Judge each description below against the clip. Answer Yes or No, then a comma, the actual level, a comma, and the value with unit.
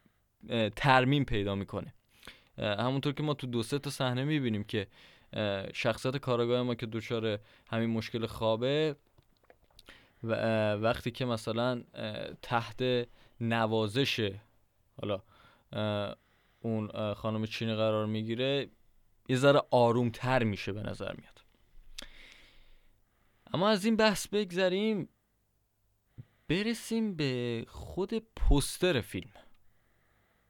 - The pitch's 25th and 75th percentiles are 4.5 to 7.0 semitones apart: No, average, 3.4 semitones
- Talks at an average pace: No, slow, 100 wpm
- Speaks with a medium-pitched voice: No, low, 115 Hz